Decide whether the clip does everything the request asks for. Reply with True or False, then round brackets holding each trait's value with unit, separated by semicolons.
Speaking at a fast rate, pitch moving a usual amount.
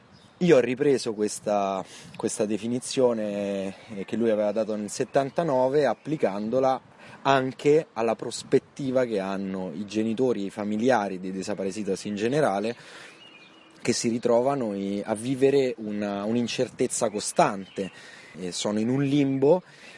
False (115 wpm; 4.3 semitones)